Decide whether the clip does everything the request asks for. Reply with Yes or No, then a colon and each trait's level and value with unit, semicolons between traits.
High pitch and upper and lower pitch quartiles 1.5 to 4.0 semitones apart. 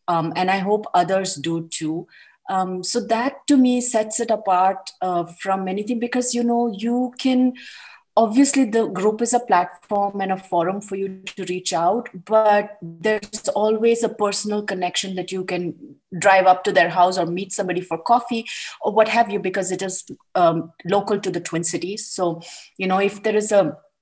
Yes: high, 195 Hz; average, 3.5 semitones